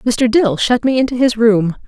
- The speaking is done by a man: No, female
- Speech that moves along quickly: Yes, fast, 225 wpm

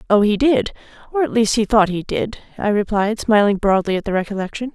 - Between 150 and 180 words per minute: No, average, 200 wpm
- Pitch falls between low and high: No, high, 215 Hz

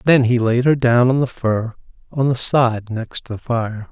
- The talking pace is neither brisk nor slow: No, fast, 215 wpm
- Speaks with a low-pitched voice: Yes, low, 120 Hz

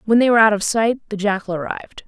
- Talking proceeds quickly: Yes, fast, 260 wpm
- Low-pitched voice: No, high, 215 Hz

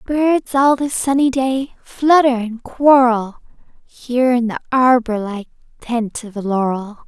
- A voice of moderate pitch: No, high, 245 Hz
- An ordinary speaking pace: Yes, average, 145 wpm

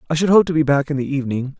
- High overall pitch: No, medium, 145 Hz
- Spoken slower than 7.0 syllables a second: No, 7.9 syllables/s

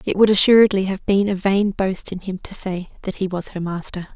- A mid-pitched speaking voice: No, high, 195 Hz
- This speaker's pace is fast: Yes, fast, 245 wpm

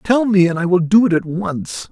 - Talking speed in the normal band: No, fast, 280 wpm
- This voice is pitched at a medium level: Yes, medium, 180 Hz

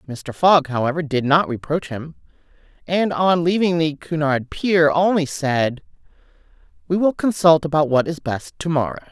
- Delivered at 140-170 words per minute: Yes, average, 160 wpm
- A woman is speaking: Yes, female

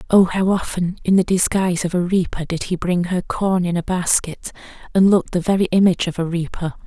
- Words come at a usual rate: No, fast, 220 wpm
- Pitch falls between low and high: Yes, medium, 180 Hz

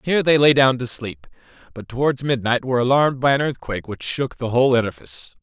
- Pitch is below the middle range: Yes, low, 130 Hz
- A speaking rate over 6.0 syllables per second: Yes, 6.4 syllables/s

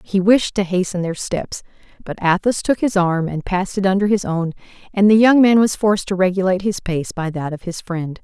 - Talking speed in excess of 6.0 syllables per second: No, 5.5 syllables/s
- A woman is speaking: Yes, female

